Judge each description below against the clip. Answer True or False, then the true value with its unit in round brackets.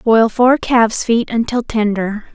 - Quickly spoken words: False (155 wpm)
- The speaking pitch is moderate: False (225 Hz)